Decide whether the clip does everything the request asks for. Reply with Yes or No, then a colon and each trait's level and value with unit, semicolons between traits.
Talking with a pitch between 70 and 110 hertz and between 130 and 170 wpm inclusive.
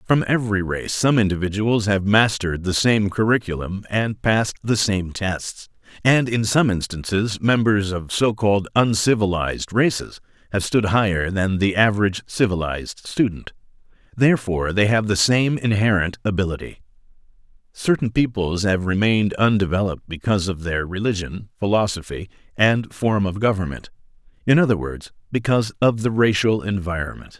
Yes: low, 105 Hz; slow, 135 wpm